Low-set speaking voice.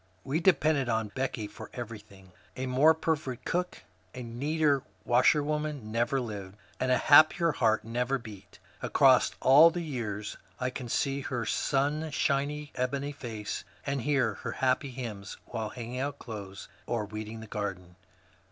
Yes: low, 125 Hz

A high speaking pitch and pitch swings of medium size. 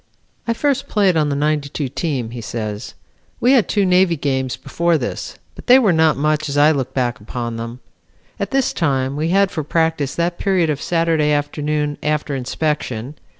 No: medium, 150 Hz; average, 4.0 semitones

